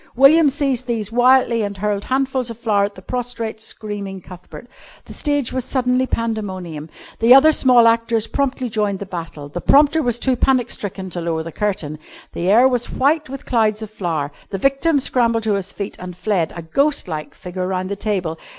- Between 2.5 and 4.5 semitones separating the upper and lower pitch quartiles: No, average, 5.3 semitones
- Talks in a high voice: Yes, high, 220 Hz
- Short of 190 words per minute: No, average, 195 wpm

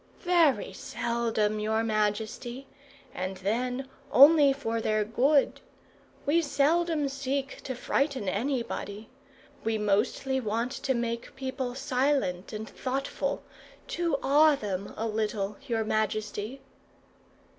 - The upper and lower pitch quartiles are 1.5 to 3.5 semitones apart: No, average, 4.3 semitones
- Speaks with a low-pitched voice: No, high, 240 Hz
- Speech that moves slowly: Yes, slow, 110 wpm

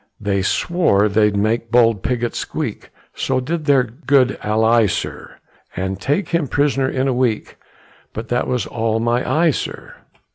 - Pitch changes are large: No, average, 3.7 semitones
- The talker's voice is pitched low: Yes, low, 120 Hz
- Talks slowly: No, average, 155 wpm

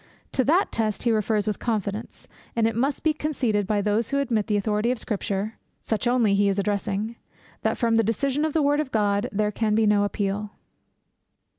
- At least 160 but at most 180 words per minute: No, average, 200 wpm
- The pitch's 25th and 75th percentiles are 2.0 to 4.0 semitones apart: Yes, average, 2.8 semitones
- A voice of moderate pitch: No, high, 220 Hz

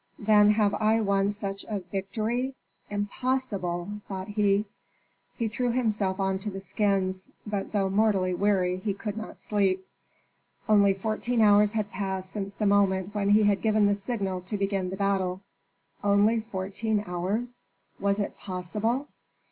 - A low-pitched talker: No, high, 205 Hz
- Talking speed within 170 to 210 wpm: No, average, 150 wpm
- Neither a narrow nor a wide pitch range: No, narrow, 1.9 semitones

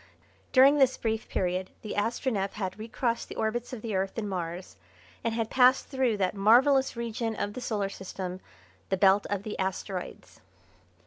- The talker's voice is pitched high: Yes, high, 215 Hz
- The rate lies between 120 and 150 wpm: No, average, 170 wpm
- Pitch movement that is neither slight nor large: Yes, average, 3.7 semitones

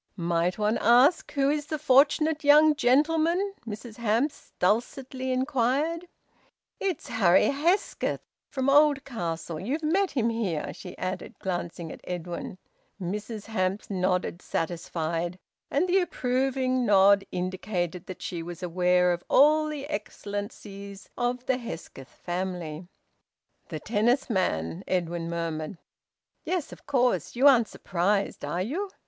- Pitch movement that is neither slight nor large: No, wide, 7.5 semitones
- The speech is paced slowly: Yes, slow, 125 wpm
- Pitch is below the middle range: No, high, 215 Hz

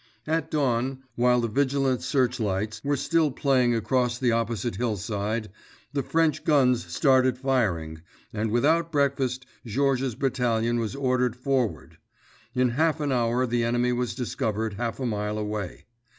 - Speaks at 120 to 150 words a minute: Yes, average, 140 wpm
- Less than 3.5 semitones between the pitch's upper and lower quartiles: Yes, average, 3.1 semitones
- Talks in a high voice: No, low, 125 Hz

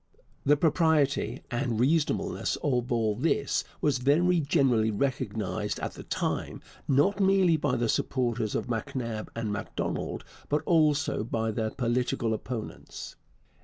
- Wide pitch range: No, average, 4.9 semitones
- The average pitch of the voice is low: Yes, low, 130 Hz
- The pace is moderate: No, slow, 130 wpm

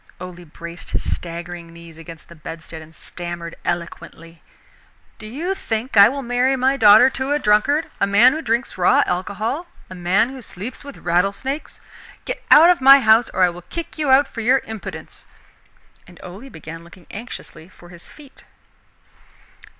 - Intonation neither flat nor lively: No, wide, 7.3 semitones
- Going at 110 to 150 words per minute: No, average, 175 wpm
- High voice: Yes, high, 205 Hz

